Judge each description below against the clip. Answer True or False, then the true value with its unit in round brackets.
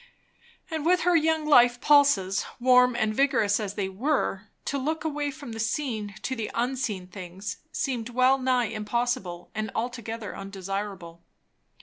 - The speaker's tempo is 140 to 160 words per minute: True (145 wpm)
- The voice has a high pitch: True (235 Hz)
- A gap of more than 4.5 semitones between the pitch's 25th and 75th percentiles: True (5.0 semitones)